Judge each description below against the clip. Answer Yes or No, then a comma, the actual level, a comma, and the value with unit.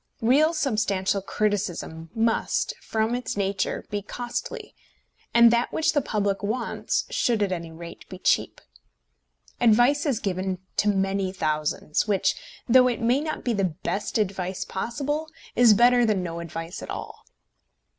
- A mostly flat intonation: No, average, 4.2 semitones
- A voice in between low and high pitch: No, high, 210 Hz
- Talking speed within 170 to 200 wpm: No, average, 145 wpm